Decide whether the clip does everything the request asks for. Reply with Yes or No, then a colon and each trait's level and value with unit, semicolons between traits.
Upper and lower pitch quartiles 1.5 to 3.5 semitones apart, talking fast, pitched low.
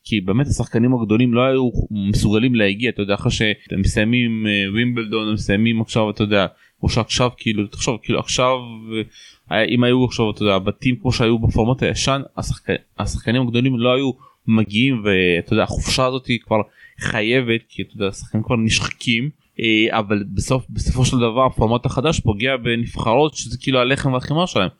Yes: average, 2.9 semitones; fast, 160 wpm; low, 115 Hz